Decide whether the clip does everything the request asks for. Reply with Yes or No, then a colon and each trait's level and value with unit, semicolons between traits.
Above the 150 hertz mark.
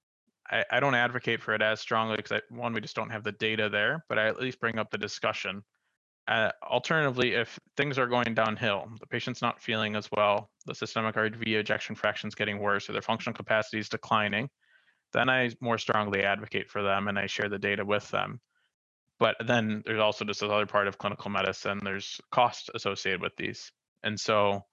No: low, 110 Hz